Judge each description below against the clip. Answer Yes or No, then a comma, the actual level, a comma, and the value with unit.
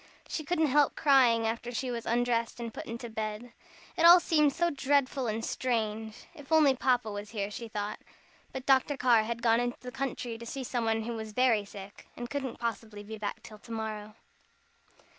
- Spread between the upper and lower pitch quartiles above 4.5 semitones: No, average, 3.1 semitones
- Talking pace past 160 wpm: Yes, average, 195 wpm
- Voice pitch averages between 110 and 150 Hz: No, high, 235 Hz